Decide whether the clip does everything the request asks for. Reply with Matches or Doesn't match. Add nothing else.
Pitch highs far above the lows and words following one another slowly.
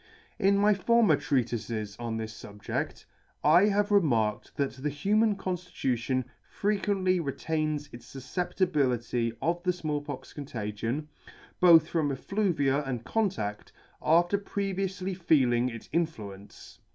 Matches